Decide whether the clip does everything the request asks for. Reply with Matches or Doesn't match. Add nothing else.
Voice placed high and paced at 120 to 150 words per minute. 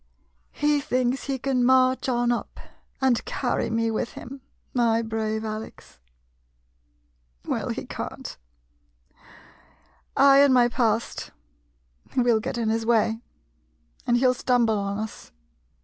Matches